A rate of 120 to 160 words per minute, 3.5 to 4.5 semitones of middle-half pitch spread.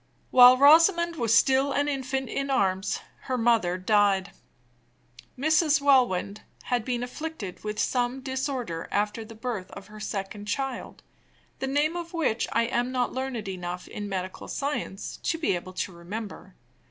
No: average, 155 wpm; average, 5.1 semitones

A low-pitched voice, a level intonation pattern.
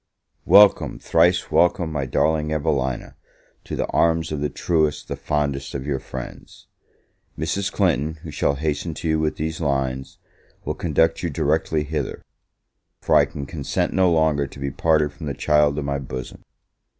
Yes: very low, 75 Hz; narrow, 2.3 semitones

